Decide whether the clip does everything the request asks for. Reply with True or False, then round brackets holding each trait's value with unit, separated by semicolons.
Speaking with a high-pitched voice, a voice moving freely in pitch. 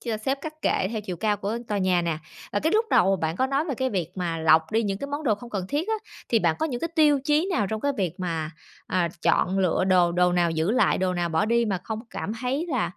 True (205 Hz; 6.7 semitones)